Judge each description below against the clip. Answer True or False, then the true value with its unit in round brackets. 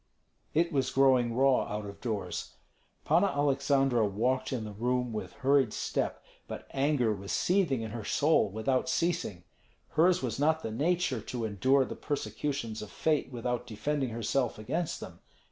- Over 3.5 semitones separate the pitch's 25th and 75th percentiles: True (4.6 semitones)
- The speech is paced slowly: False (160 wpm)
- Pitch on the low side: True (130 Hz)